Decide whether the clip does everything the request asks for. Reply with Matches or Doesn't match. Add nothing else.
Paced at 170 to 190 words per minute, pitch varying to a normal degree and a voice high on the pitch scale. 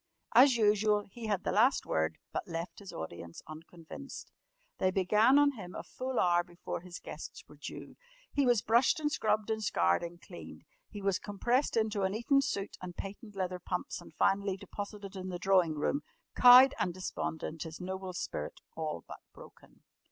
Matches